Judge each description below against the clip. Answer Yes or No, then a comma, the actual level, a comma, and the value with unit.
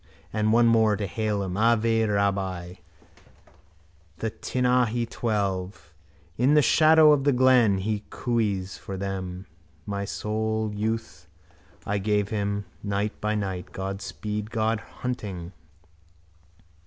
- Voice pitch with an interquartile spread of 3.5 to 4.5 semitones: No, narrow, 2.6 semitones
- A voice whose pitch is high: No, low, 105 Hz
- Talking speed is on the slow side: Yes, slow, 120 wpm